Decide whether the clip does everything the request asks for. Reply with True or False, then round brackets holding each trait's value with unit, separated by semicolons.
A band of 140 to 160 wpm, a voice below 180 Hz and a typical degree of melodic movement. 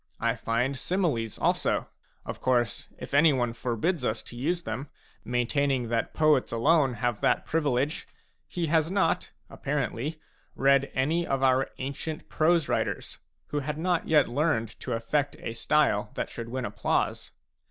True (150 wpm; 135 Hz; 4.2 semitones)